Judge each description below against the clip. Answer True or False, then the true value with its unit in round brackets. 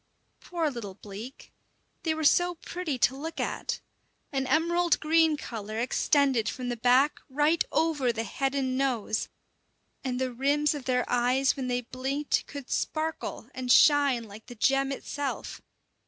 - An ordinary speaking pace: True (155 wpm)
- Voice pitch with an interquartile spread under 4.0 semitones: True (3.3 semitones)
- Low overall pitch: False (270 Hz)